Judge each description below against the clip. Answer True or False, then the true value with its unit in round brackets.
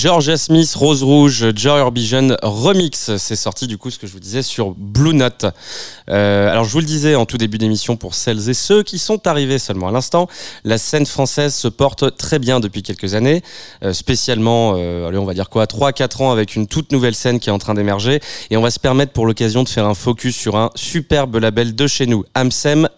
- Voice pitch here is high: False (125 Hz)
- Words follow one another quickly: True (230 wpm)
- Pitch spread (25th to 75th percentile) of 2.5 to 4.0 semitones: False (4.8 semitones)